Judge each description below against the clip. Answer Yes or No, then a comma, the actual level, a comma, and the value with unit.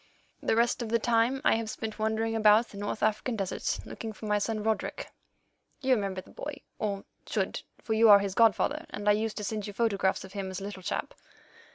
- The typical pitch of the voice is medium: No, high, 215 Hz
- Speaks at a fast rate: Yes, fast, 220 wpm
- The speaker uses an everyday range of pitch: No, narrow, 2.0 semitones